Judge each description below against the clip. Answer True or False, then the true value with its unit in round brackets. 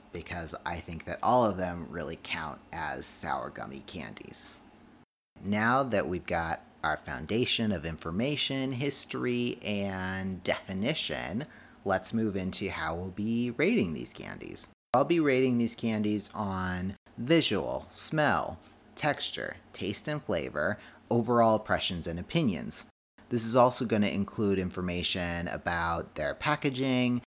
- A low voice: True (105 Hz)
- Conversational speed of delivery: False (125 wpm)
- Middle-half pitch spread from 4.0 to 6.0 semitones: True (5.5 semitones)